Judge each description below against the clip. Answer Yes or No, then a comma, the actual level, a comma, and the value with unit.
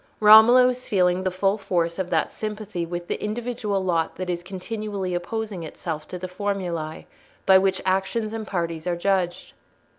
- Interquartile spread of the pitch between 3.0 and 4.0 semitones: Yes, average, 3.3 semitones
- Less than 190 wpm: Yes, average, 170 wpm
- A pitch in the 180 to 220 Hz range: Yes, high, 190 Hz